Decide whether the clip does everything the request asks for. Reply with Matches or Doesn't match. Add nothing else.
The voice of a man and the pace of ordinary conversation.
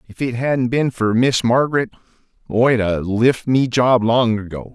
Matches